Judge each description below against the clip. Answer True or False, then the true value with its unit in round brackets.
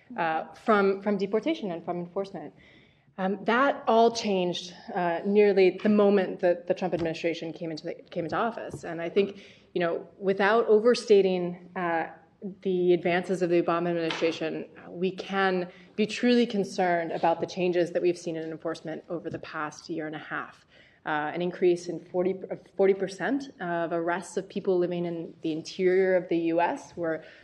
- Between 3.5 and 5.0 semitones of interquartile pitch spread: False (2.8 semitones)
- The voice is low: False (180 Hz)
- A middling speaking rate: True (170 wpm)